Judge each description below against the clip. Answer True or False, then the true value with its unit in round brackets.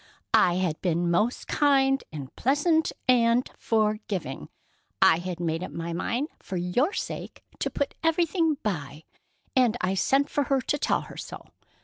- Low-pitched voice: False (225 Hz)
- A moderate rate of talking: True (155 wpm)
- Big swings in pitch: True (8.0 semitones)